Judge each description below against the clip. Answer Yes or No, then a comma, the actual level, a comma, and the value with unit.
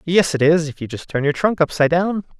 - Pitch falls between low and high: Yes, medium, 160 Hz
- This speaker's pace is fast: Yes, fast, 275 wpm